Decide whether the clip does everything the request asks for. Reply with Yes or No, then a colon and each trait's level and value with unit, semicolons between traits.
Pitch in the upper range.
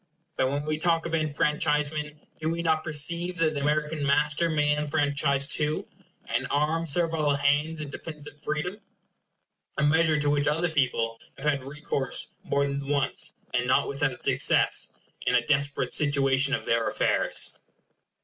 No: medium, 150 Hz